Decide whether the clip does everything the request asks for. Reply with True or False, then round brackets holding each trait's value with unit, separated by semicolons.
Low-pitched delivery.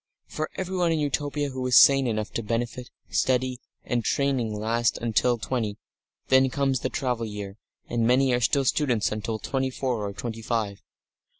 True (125 Hz)